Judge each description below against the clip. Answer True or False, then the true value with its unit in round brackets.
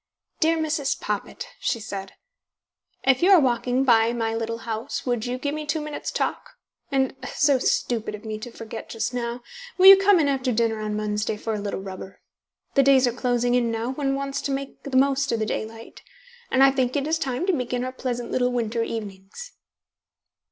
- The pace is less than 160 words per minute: False (200 wpm)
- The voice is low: False (245 Hz)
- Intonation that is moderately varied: True (3.5 semitones)